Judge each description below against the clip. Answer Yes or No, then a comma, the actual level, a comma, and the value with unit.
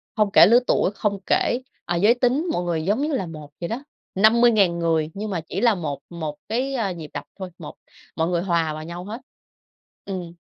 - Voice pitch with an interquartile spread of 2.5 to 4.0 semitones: No, average, 5.2 semitones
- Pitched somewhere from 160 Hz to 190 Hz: Yes, medium, 185 Hz